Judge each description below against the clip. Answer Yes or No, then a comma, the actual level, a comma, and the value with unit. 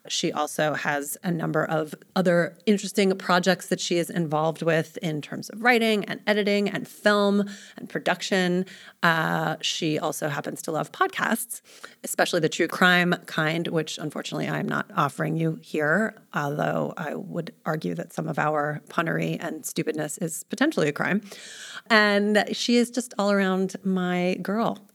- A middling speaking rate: Yes, average, 160 wpm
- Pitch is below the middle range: No, medium, 185 Hz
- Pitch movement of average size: Yes, average, 4.6 semitones